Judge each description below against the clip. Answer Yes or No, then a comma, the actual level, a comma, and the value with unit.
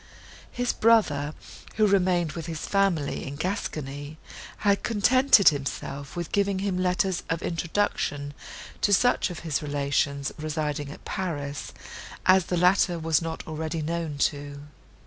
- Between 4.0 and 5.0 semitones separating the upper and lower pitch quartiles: Yes, average, 4.7 semitones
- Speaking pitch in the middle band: Yes, medium, 165 Hz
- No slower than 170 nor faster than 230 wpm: No, slow, 135 wpm